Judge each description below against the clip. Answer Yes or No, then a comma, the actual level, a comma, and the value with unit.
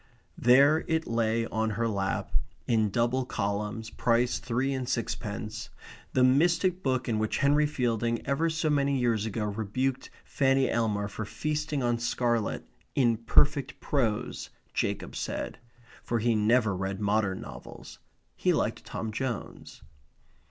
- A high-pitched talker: No, low, 120 Hz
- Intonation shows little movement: No, average, 3.7 semitones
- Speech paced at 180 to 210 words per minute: No, average, 140 wpm